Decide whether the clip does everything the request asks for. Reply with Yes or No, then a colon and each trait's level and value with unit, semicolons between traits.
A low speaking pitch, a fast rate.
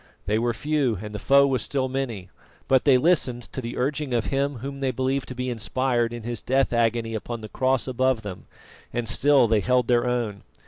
Yes: low, 125 Hz; fast, 215 wpm